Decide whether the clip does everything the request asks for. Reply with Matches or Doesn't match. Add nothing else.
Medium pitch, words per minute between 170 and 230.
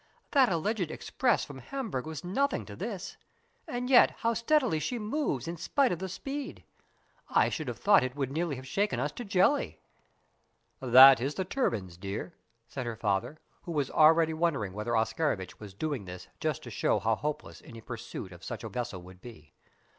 Matches